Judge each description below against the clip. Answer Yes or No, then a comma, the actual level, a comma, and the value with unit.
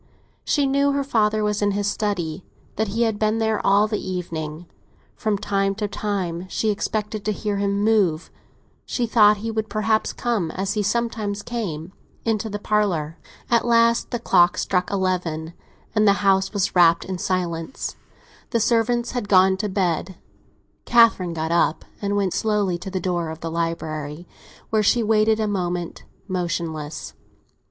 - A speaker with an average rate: Yes, average, 160 wpm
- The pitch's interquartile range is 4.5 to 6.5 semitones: No, average, 3.6 semitones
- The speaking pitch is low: No, high, 200 Hz